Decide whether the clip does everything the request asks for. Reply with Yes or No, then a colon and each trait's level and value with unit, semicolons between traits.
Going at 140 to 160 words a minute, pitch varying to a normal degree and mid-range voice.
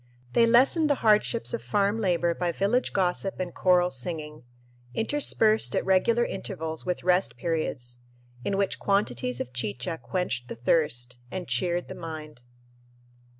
Yes: average, 145 wpm; average, 4.9 semitones; medium, 180 Hz